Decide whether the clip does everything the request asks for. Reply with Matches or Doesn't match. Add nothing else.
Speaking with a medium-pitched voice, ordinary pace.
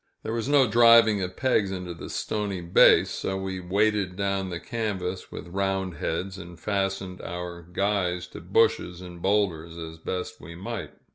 Doesn't match